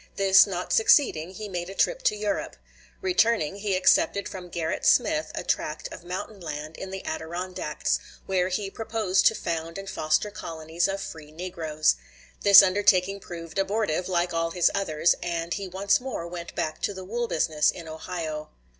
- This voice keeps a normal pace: Yes, average, 170 wpm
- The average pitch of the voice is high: No, medium, 180 Hz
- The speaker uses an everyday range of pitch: Yes, average, 3.2 semitones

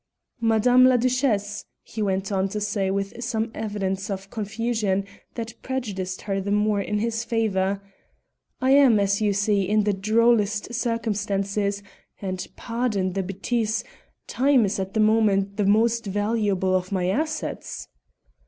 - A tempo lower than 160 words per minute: Yes, average, 145 wpm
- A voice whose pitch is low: No, high, 210 Hz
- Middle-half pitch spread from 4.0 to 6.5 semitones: No, average, 2.7 semitones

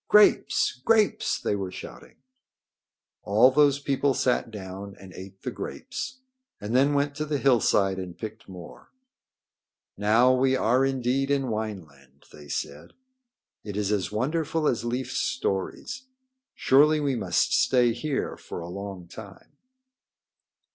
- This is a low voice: Yes, low, 120 Hz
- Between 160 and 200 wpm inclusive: No, slow, 135 wpm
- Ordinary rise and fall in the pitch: No, wide, 5.9 semitones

